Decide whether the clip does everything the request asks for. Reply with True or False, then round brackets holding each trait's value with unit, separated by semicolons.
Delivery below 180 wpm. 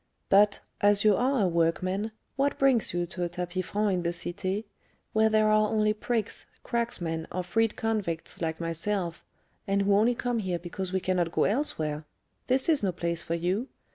False (185 wpm)